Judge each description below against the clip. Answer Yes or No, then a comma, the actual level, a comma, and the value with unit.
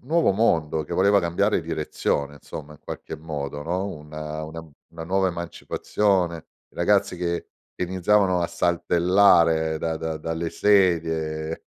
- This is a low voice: Yes, very low, 85 Hz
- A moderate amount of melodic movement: Yes, average, 3.0 semitones